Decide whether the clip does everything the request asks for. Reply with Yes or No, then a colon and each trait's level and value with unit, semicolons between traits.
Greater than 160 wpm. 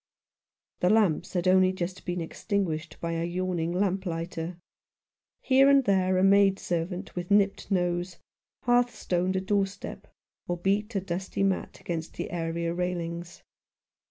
No: slow, 135 wpm